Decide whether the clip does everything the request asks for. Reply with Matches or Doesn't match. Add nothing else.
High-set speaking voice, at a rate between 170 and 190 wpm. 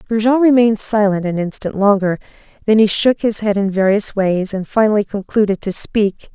Matches